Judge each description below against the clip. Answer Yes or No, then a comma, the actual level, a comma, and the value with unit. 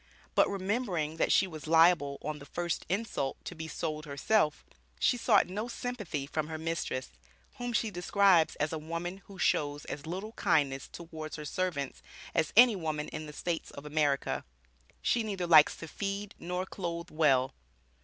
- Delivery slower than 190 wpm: Yes, average, 170 wpm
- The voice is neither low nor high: Yes, medium, 165 Hz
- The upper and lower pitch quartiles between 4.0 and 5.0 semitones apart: Yes, average, 4.3 semitones